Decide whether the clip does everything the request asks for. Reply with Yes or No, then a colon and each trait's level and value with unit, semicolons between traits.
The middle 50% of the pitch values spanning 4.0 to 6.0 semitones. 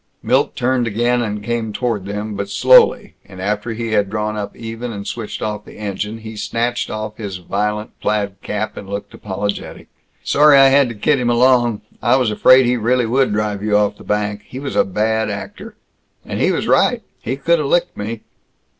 No: average, 2.9 semitones